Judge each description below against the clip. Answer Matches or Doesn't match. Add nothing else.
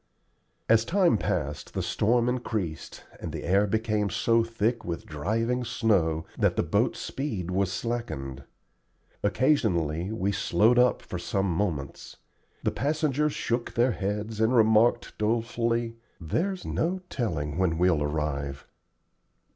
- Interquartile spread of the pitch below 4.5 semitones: Doesn't match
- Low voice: Matches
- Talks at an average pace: Doesn't match